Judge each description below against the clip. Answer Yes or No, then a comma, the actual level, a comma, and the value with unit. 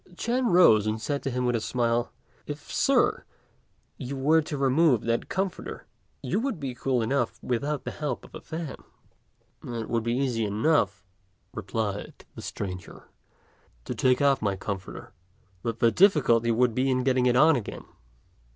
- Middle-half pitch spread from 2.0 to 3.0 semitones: No, average, 4.1 semitones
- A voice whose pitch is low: Yes, low, 125 Hz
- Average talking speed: Yes, average, 165 wpm